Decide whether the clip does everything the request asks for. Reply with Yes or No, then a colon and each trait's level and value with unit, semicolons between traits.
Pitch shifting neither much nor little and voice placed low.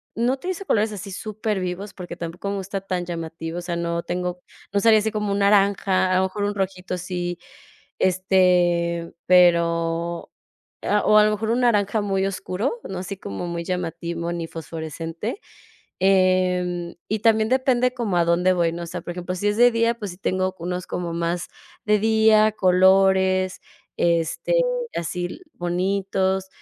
No: average, 3.0 semitones; medium, 185 Hz